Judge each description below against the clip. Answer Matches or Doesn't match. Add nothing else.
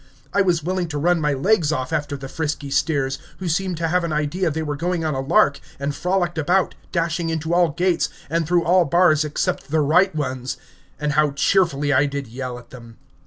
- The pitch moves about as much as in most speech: Matches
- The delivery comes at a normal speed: Doesn't match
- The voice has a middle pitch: Matches